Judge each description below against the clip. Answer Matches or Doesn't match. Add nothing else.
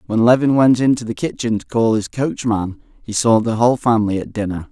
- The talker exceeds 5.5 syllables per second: Matches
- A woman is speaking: Doesn't match